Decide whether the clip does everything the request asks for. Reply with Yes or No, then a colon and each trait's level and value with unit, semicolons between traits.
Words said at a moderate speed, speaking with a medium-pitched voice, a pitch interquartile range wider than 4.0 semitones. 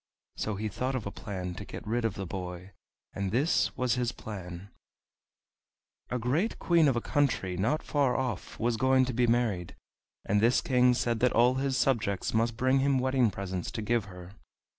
No: average, 190 wpm; low, 115 Hz; average, 4.6 semitones